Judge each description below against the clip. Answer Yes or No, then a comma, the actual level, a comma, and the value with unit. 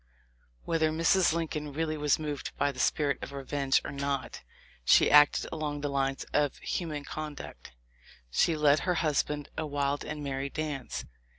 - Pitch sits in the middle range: Yes, medium, 145 Hz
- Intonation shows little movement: Yes, narrow, 1.8 semitones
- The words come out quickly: No, average, 165 wpm